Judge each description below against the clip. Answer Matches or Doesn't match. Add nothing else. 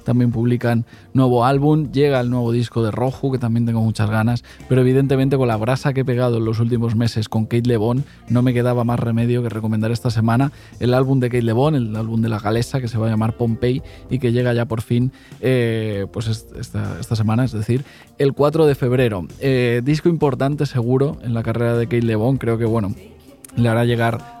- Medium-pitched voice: Doesn't match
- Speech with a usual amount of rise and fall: Doesn't match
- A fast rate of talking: Matches